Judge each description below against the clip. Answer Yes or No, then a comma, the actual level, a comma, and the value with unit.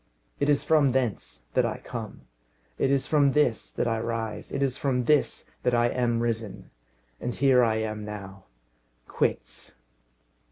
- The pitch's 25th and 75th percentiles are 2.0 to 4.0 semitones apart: Yes, average, 3.6 semitones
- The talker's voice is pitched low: Yes, low, 120 Hz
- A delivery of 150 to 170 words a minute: Yes, average, 160 wpm